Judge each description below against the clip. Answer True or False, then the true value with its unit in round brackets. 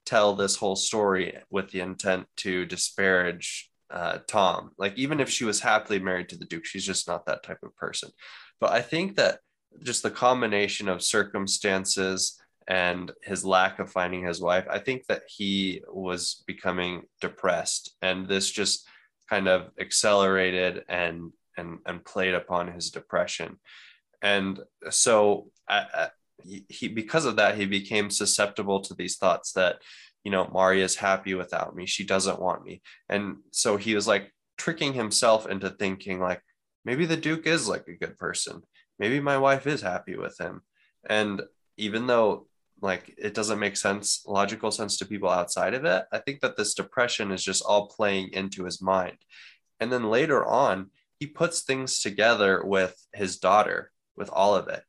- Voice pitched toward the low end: True (100 Hz)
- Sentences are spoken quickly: False (175 wpm)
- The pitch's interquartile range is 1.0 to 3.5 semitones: True (2.5 semitones)